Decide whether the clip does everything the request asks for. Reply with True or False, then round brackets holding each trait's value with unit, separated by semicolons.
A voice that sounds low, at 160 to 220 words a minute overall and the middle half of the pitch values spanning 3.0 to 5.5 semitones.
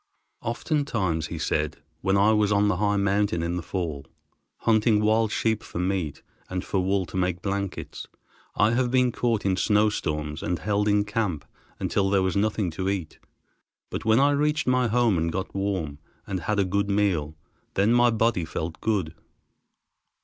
True (100 Hz; 175 wpm; 3.5 semitones)